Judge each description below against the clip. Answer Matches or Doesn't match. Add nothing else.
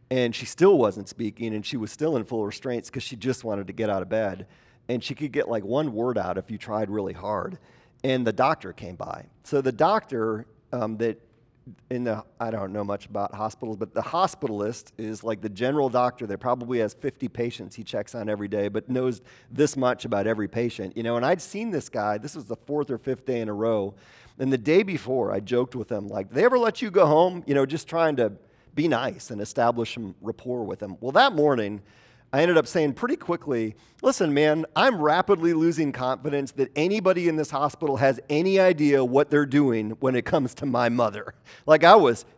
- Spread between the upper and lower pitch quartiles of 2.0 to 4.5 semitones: Doesn't match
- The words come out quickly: Matches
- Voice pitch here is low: Matches